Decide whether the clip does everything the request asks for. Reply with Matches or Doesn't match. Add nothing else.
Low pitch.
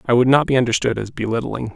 Matches